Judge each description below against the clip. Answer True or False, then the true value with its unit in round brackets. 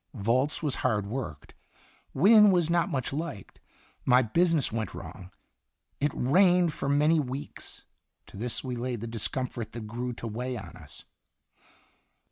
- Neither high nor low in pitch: False (130 Hz)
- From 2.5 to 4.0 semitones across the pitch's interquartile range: False (5.2 semitones)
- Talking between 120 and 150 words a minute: True (145 wpm)